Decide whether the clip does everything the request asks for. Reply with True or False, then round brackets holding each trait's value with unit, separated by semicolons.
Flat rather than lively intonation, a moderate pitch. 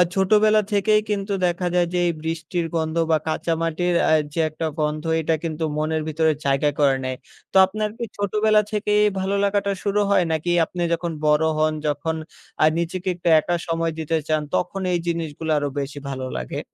False (3.8 semitones; 165 Hz)